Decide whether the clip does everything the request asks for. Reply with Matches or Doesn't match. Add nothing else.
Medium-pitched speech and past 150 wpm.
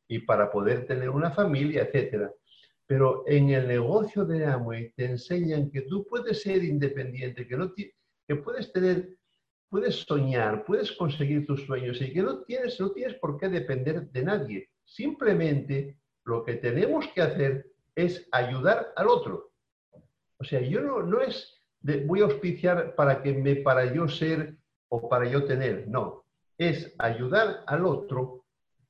Matches